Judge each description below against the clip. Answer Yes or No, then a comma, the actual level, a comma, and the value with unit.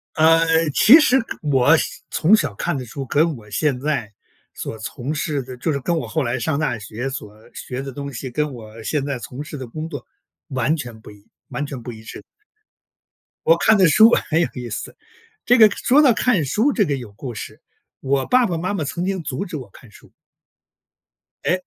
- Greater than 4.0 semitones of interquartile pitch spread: Yes, average, 5.2 semitones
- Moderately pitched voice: Yes, medium, 145 Hz